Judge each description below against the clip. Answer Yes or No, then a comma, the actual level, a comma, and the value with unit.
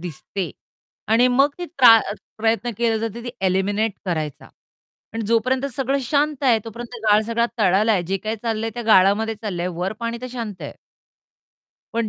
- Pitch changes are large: No, average, 3.0 semitones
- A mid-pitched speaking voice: No, high, 225 Hz